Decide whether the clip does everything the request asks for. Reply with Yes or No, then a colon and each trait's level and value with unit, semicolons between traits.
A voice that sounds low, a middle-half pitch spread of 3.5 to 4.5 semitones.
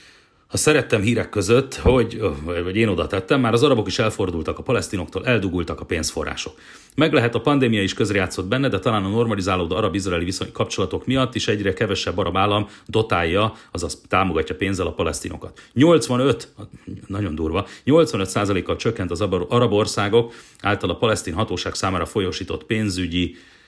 Yes: low, 105 Hz; average, 3.8 semitones